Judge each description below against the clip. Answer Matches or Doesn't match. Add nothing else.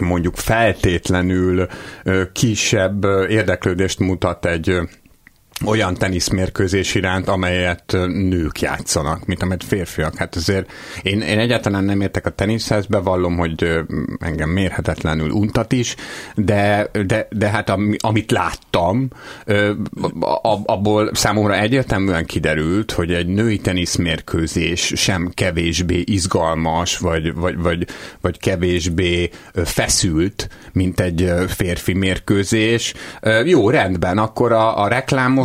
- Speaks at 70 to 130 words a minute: Matches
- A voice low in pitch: Matches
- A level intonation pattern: Doesn't match